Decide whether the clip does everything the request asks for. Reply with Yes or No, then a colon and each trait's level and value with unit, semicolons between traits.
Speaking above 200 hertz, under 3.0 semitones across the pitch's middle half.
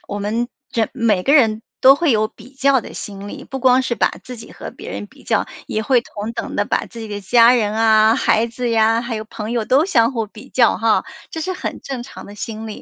Yes: high, 230 Hz; narrow, 2.6 semitones